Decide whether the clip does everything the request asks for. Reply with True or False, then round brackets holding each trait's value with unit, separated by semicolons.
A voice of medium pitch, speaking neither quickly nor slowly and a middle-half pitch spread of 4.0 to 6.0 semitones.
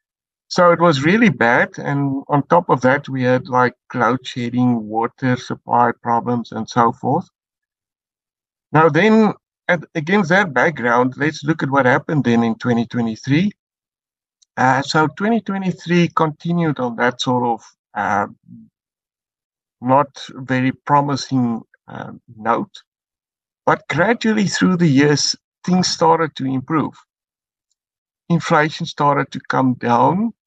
False (145 Hz; 125 wpm; 5.5 semitones)